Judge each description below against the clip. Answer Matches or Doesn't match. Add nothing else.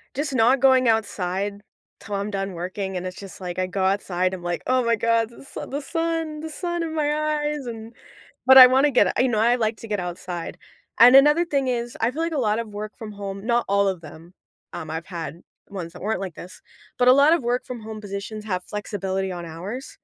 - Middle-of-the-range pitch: Doesn't match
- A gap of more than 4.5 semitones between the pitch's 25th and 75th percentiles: Matches